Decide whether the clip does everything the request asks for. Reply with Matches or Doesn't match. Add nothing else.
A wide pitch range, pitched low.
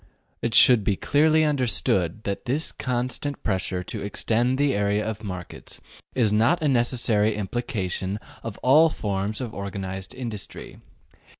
Doesn't match